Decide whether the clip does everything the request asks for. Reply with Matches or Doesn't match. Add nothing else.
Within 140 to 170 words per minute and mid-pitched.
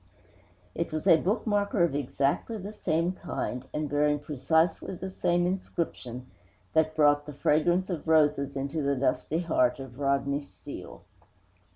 Matches